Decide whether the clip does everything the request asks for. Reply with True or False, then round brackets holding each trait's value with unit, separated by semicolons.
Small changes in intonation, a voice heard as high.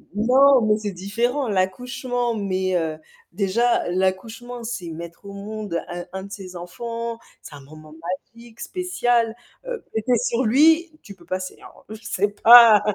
False (4.4 semitones; 215 Hz)